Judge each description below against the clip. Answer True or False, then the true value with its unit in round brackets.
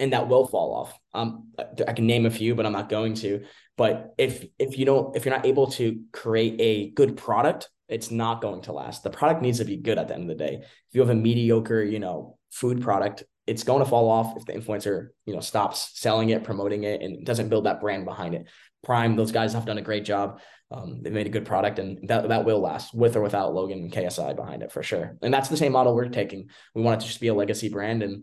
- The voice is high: False (115 Hz)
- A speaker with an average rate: False (265 wpm)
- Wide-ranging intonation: False (2.4 semitones)